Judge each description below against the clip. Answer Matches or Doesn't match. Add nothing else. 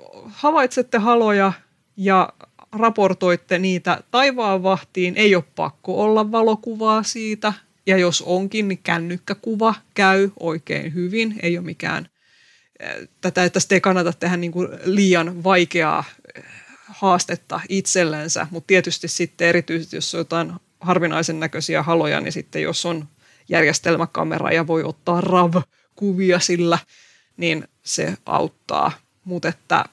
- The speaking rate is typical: Matches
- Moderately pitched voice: Matches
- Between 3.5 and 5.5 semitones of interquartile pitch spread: Doesn't match